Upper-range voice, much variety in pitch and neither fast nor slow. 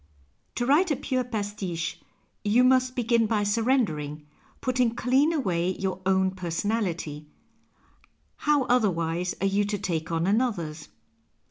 No: high, 205 Hz; wide, 6.3 semitones; slow, 130 wpm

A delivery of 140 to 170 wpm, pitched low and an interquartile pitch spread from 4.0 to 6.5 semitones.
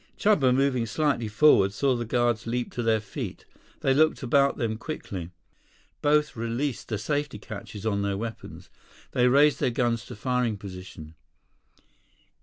Yes: average, 150 wpm; low, 120 Hz; average, 4.3 semitones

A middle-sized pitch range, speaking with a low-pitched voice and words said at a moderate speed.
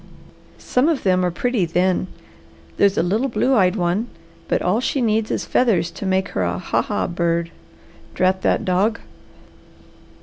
No: average, 4.2 semitones; high, 190 Hz; average, 165 wpm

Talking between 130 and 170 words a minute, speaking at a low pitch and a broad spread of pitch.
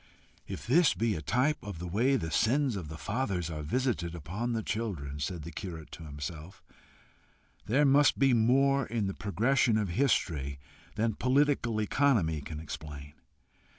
Yes: average, 160 wpm; low, 105 Hz; wide, 8.0 semitones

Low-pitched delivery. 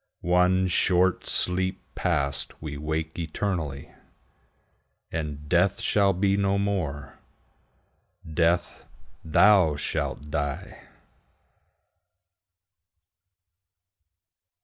Yes: very low, 85 Hz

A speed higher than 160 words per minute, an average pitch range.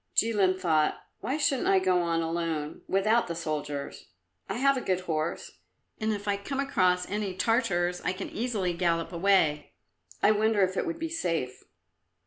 Yes: average, 170 wpm; average, 4.5 semitones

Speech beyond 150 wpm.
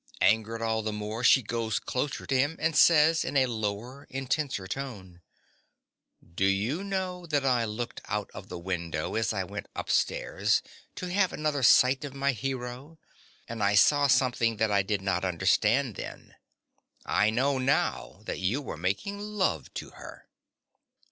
Yes: average, 160 wpm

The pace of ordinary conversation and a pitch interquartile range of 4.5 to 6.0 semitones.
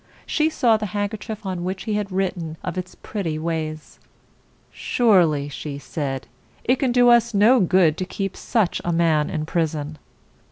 Yes: average, 165 wpm; average, 5.2 semitones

